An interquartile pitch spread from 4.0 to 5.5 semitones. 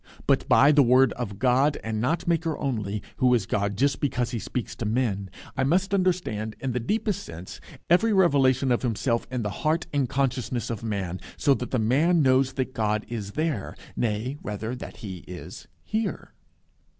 Yes: average, 4.8 semitones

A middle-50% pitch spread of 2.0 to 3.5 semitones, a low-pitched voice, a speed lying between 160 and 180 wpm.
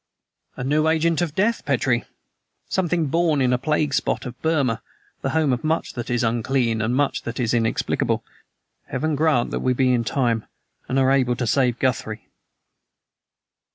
No: average, 4.3 semitones; low, 130 Hz; average, 170 wpm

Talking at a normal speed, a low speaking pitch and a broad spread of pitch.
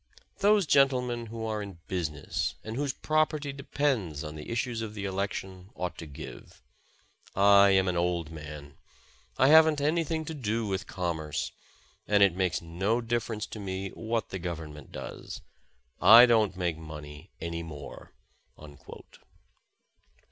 Yes: average, 150 wpm; low, 100 Hz; wide, 6.1 semitones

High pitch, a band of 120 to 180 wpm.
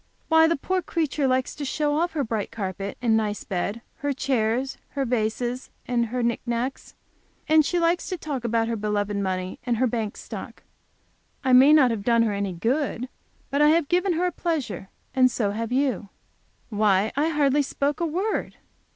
No: very high, 250 Hz; average, 190 wpm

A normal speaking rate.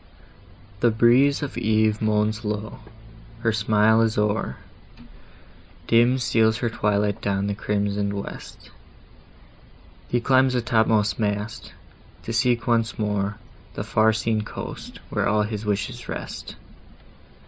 No: slow, 125 wpm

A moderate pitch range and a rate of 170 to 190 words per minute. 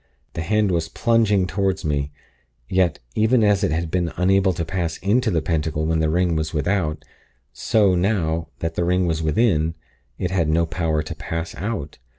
Yes: average, 3.5 semitones; average, 180 wpm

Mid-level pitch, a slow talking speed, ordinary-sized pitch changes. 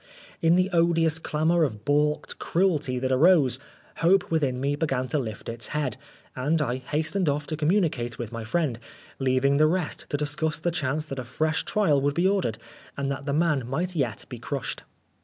No: medium, 150 Hz; average, 190 wpm; average, 4.1 semitones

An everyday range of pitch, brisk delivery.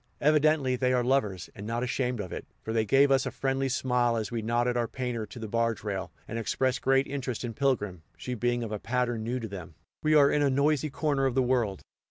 Yes: average, 3.0 semitones; fast, 240 wpm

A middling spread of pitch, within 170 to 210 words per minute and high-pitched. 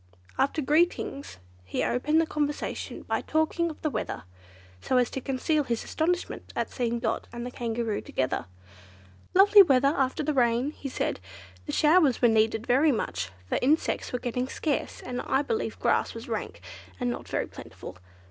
Yes: average, 4.4 semitones; average, 175 wpm; very high, 265 Hz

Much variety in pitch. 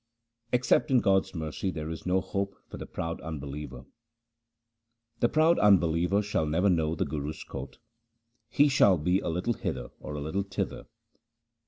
Yes: wide, 5.7 semitones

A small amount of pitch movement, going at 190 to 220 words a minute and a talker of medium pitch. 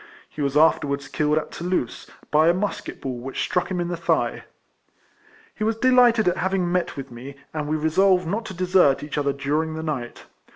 No: average, 4.4 semitones; average, 200 wpm; medium, 160 Hz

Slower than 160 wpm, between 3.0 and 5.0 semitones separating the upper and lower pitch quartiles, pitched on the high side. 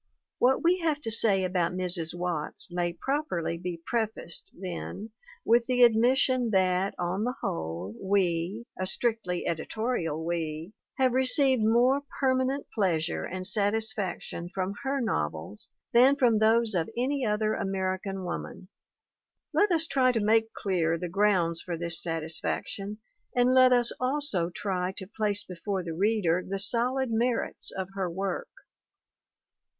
No: average, 145 wpm; wide, 5.5 semitones; high, 200 Hz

